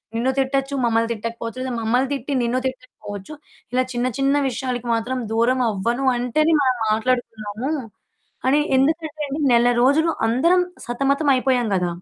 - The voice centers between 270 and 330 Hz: No, very high, 255 Hz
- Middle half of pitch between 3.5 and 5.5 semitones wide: No, average, 2.8 semitones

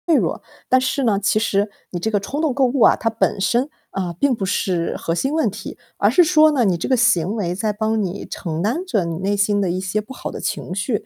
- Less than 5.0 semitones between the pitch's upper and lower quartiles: No, average, 5.3 semitones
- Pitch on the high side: Yes, high, 210 Hz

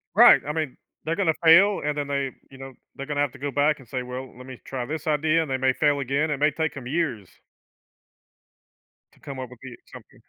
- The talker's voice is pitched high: No, medium, 140 Hz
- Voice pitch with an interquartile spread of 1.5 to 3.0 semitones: Yes, average, 2.7 semitones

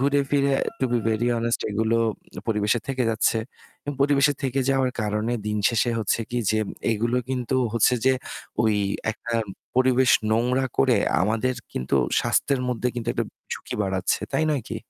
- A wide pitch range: No, average, 3.1 semitones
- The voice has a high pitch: No, low, 120 Hz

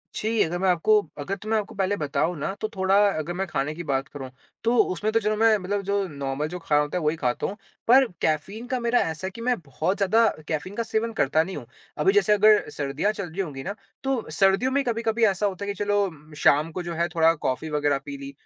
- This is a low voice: No, high, 190 Hz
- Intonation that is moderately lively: No, wide, 5.7 semitones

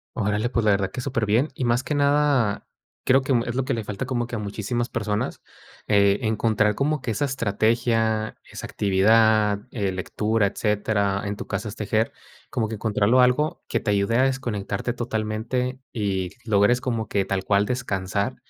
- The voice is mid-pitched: No, low, 110 Hz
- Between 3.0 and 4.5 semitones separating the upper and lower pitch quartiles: Yes, average, 3.3 semitones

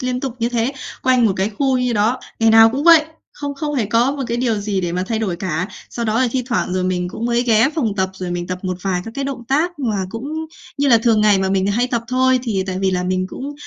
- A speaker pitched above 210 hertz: Yes, high, 230 Hz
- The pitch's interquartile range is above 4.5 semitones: Yes, average, 5.0 semitones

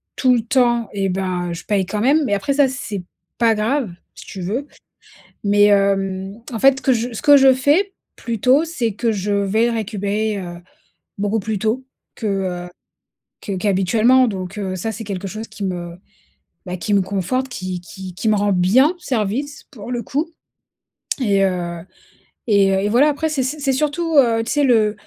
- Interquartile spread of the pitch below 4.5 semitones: No, average, 4.9 semitones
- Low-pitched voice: No, high, 215 Hz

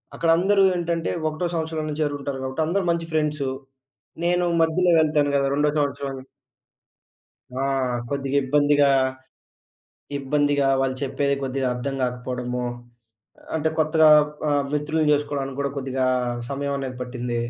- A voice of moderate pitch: Yes, medium, 145 Hz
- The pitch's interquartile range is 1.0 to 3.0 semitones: Yes, average, 2.7 semitones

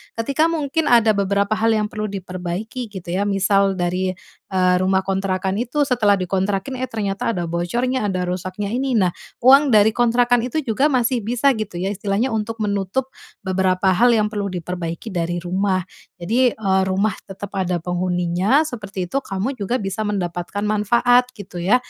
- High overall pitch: Yes, high, 200 Hz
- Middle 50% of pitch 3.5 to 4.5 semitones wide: Yes, average, 4.2 semitones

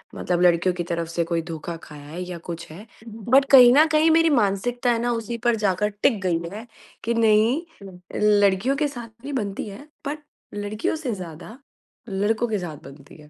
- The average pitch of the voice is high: Yes, high, 210 Hz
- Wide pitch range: Yes, wide, 5.7 semitones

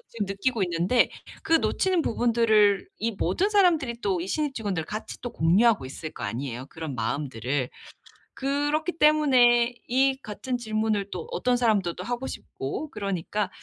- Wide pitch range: Yes, wide, 6.4 semitones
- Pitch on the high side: Yes, high, 220 Hz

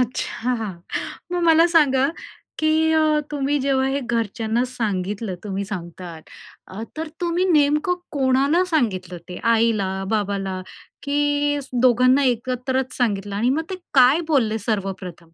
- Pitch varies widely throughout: Yes, wide, 5.9 semitones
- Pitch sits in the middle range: No, very high, 250 Hz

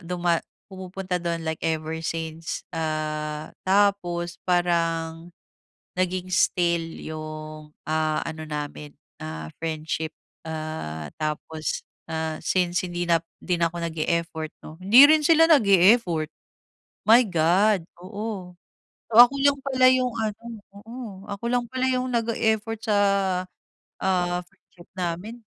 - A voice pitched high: No, medium, 175 Hz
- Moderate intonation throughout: Yes, average, 4.3 semitones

